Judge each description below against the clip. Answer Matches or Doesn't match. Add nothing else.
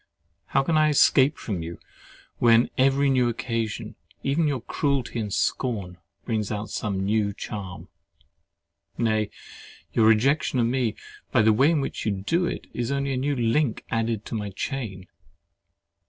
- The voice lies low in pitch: Matches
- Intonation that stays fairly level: Doesn't match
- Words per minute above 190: Doesn't match